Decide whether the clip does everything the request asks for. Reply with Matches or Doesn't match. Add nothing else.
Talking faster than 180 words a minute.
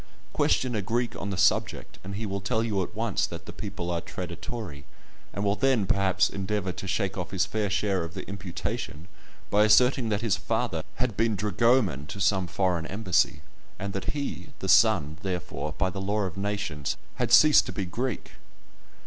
Matches